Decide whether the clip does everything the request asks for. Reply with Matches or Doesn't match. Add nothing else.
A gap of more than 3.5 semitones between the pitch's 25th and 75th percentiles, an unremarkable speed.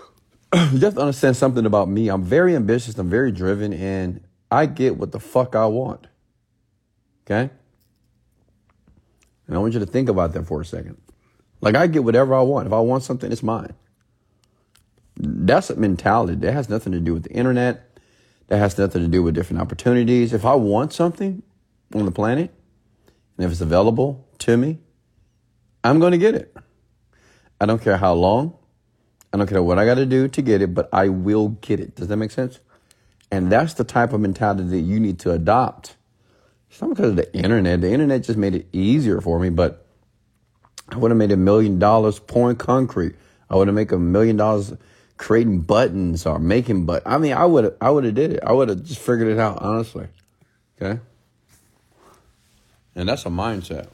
Matches